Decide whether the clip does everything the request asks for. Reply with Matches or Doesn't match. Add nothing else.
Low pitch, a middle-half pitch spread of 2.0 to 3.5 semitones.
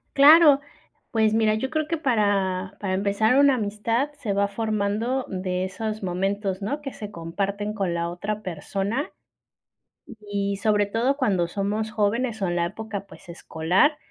Doesn't match